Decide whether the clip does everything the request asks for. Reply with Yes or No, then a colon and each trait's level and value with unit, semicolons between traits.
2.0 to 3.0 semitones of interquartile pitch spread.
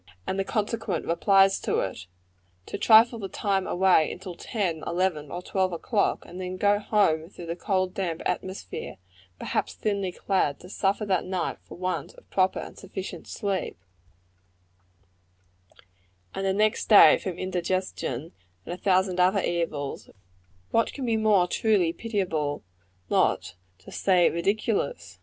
Yes: narrow, 2.6 semitones